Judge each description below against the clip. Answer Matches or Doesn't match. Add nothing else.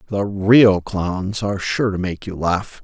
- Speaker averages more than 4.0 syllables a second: Doesn't match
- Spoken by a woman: Doesn't match